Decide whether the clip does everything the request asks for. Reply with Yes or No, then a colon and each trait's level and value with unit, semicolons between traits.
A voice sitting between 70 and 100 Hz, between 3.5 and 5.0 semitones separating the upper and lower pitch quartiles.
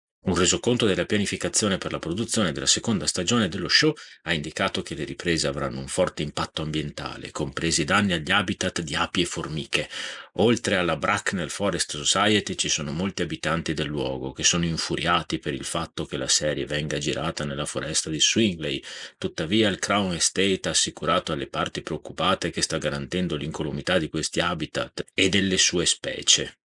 Yes: very low, 90 Hz; average, 4.0 semitones